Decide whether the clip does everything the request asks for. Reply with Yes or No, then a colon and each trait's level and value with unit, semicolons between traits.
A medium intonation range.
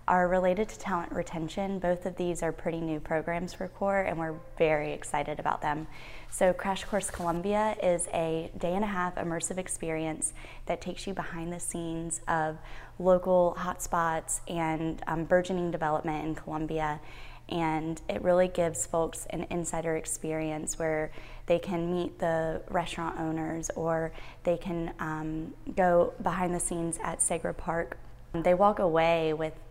No: narrow, 2.0 semitones